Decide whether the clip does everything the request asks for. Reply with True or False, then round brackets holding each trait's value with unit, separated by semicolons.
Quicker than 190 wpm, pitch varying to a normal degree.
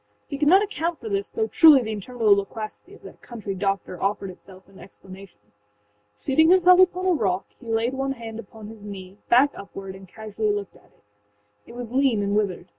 False (200 wpm; 5.9 semitones)